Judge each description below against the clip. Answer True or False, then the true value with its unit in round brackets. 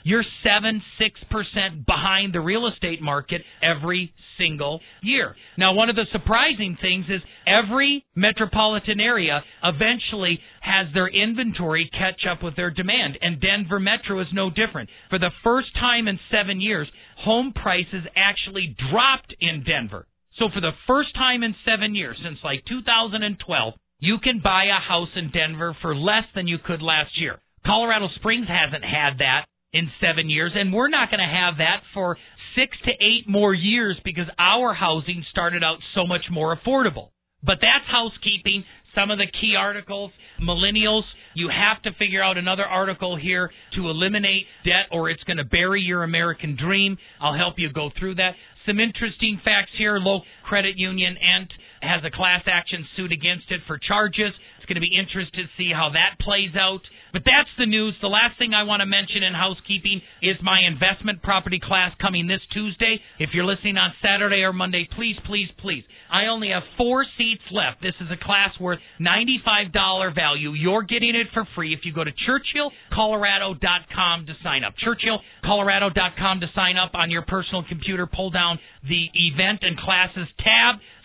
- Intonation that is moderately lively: True (3.4 semitones)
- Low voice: False (190 Hz)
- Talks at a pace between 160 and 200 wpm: True (175 wpm)